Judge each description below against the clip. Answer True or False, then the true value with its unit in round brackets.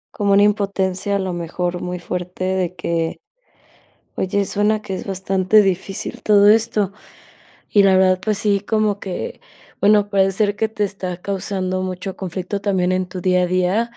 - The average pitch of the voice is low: False (190 Hz)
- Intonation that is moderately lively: False (1.9 semitones)